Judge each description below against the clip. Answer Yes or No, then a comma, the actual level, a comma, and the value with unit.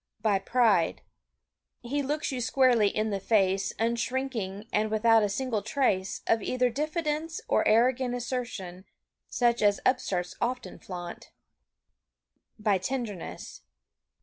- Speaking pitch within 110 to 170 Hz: No, high, 230 Hz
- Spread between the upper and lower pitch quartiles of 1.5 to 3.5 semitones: No, average, 4.2 semitones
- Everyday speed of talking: No, slow, 120 wpm